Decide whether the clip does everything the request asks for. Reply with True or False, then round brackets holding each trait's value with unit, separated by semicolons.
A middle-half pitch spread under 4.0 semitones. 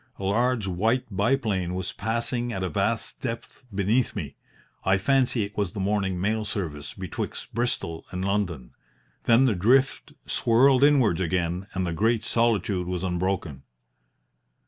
False (4.4 semitones)